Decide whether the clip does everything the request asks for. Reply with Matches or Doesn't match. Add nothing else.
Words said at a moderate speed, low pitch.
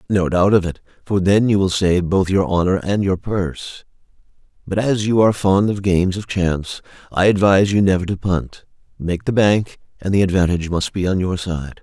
Doesn't match